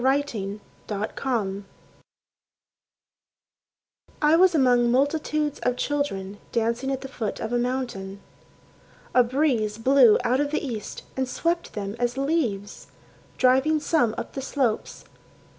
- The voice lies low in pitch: No, very high, 255 Hz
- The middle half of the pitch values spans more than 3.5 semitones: Yes, average, 4.5 semitones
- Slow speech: Yes, slow, 125 wpm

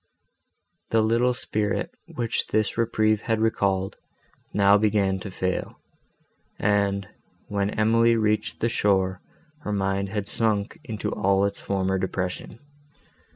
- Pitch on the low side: Yes, low, 105 Hz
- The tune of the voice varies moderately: No, narrow, 2.1 semitones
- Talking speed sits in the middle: No, slow, 120 wpm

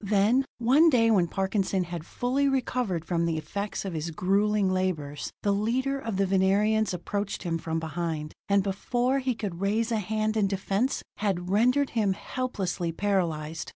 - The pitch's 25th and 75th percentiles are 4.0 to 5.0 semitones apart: Yes, average, 4.4 semitones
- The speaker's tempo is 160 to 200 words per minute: Yes, average, 165 wpm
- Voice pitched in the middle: No, high, 200 Hz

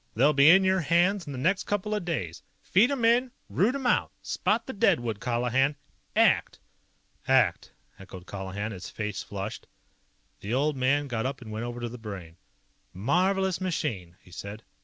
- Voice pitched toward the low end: Yes, low, 130 Hz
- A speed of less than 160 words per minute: No, average, 175 wpm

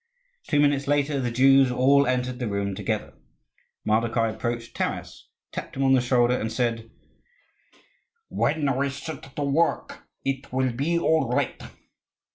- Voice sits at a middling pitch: No, low, 130 Hz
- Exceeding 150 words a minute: No, average, 145 wpm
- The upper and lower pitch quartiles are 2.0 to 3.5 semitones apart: Yes, average, 2.7 semitones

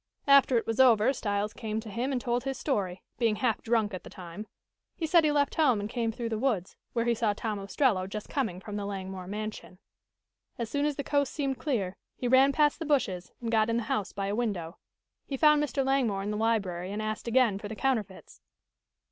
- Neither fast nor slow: No, fast, 225 wpm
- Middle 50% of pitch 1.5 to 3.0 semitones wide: No, average, 4.5 semitones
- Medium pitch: No, high, 225 Hz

